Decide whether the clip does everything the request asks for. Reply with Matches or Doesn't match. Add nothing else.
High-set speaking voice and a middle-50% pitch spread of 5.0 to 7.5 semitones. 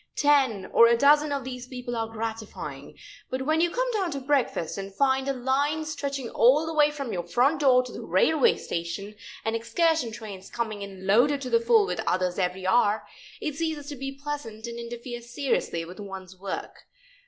Matches